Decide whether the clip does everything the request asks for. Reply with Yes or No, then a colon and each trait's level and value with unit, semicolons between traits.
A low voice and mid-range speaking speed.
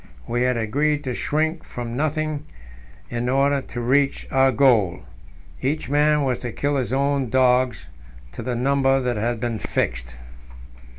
Yes: low, 130 Hz; average, 155 wpm